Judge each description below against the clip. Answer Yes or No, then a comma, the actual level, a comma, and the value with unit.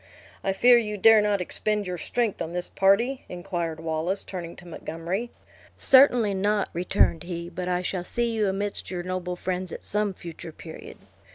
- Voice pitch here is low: No, medium, 185 Hz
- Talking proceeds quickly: No, average, 175 wpm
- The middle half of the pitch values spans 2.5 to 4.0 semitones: Yes, average, 3.1 semitones